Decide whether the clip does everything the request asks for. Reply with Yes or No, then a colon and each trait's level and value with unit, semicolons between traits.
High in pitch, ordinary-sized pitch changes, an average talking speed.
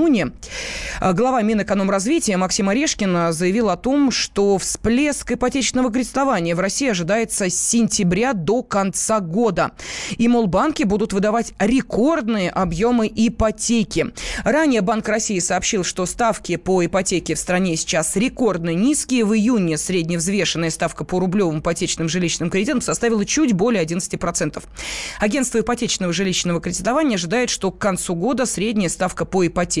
Yes: high, 200 Hz; average, 4.6 semitones; average, 135 wpm